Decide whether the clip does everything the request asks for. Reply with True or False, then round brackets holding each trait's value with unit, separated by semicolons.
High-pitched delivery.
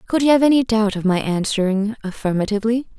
True (215 Hz)